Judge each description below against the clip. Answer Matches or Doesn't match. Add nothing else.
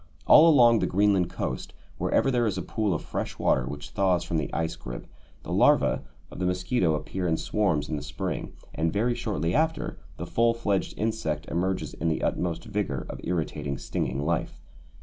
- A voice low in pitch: Matches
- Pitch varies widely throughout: Matches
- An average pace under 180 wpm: Doesn't match